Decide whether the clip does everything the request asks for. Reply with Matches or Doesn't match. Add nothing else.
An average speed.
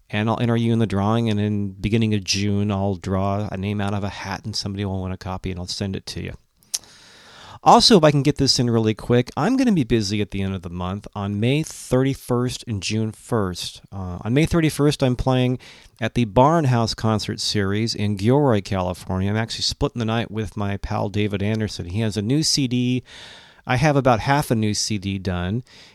Doesn't match